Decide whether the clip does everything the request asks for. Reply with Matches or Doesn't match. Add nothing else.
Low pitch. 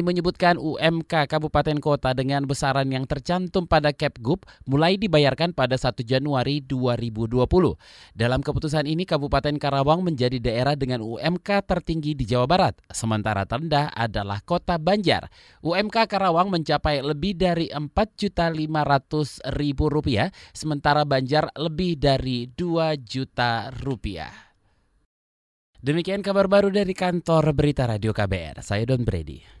Doesn't match